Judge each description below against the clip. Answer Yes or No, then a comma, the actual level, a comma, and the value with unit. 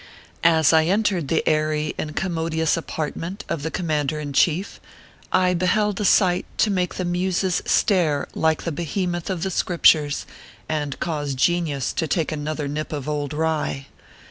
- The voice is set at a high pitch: No, medium, 160 Hz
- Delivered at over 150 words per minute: Yes, average, 165 wpm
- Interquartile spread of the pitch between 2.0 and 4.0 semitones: Yes, average, 2.9 semitones